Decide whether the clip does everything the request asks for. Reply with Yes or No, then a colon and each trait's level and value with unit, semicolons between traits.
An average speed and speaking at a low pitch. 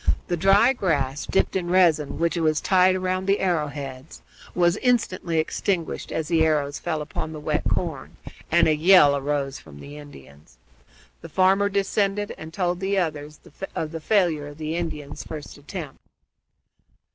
No: average, 160 wpm; medium, 160 Hz